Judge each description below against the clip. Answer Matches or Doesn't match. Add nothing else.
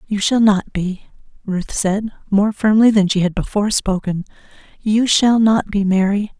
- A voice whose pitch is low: Doesn't match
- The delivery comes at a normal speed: Matches